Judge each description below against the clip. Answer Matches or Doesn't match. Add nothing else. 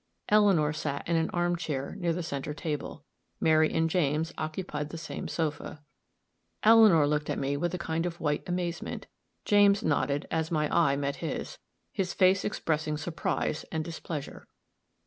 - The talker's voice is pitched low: Doesn't match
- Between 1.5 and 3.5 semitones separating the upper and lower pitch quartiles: Matches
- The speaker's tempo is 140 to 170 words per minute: Matches